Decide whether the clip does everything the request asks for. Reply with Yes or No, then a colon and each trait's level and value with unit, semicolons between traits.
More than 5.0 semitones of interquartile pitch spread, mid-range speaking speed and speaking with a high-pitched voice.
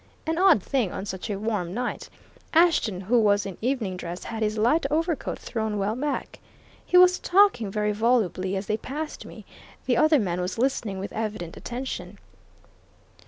Yes: wide, 5.6 semitones; average, 170 wpm; high, 220 Hz